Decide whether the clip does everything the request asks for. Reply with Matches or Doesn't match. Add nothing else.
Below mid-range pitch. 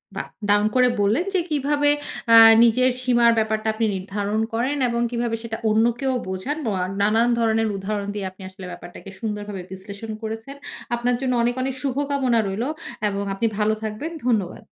Doesn't match